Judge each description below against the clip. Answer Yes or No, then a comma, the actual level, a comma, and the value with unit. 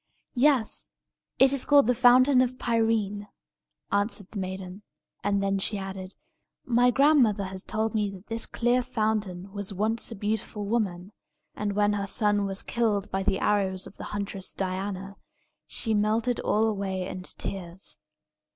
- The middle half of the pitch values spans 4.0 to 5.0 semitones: No, average, 2.8 semitones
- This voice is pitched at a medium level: No, high, 205 Hz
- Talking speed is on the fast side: No, average, 155 wpm